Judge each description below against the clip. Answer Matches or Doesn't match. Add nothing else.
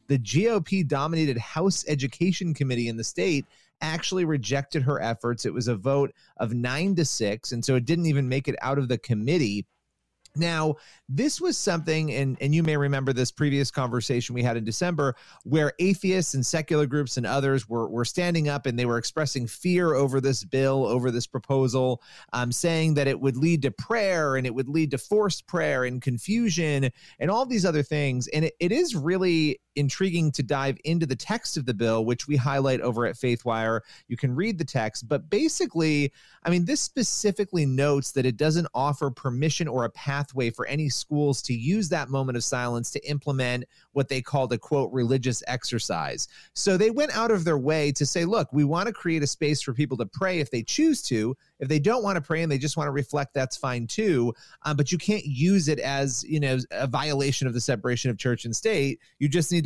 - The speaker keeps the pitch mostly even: Doesn't match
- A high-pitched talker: Doesn't match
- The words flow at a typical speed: Doesn't match